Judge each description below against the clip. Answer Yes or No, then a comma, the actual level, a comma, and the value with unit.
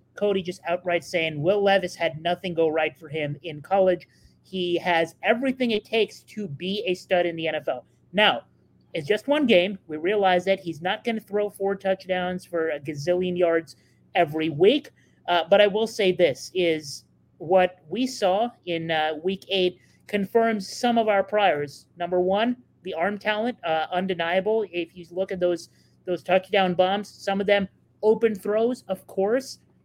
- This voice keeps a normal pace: Yes, average, 175 wpm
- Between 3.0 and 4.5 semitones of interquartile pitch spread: Yes, average, 3.3 semitones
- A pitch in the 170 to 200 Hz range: Yes, medium, 185 Hz